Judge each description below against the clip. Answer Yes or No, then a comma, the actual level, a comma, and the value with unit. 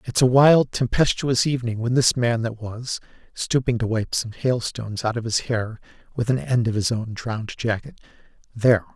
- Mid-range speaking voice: No, low, 120 Hz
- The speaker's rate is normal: Yes, average, 190 wpm